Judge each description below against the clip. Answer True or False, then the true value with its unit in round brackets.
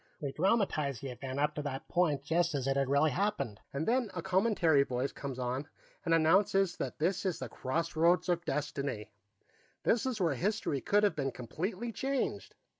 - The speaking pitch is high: False (155 Hz)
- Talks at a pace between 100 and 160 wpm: False (180 wpm)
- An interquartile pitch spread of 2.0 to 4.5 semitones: False (5.6 semitones)